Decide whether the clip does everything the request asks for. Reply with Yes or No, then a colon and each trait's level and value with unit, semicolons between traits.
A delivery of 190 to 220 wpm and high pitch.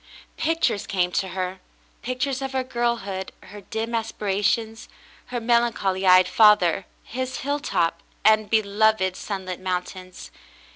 No: average, 145 wpm; high, 210 Hz